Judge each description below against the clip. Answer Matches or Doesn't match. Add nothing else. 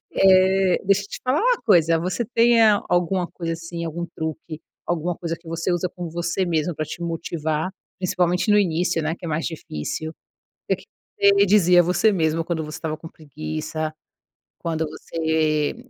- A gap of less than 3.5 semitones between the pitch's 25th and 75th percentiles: Matches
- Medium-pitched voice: Matches